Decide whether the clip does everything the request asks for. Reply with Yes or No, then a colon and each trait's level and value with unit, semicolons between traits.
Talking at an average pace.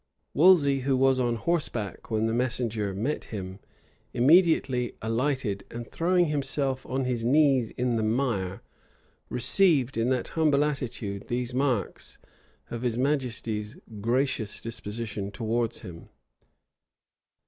No: slow, 120 wpm